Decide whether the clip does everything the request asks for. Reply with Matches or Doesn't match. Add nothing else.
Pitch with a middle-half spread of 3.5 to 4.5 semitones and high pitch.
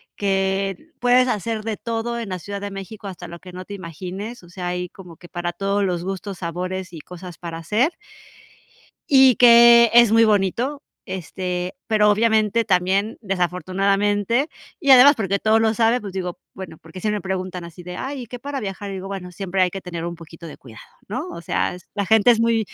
Matches